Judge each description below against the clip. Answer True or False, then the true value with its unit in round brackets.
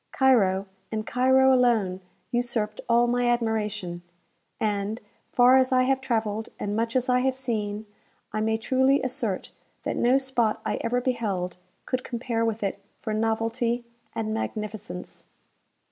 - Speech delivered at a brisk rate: False (145 wpm)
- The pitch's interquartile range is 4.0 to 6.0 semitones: False (2.8 semitones)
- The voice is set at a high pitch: True (230 Hz)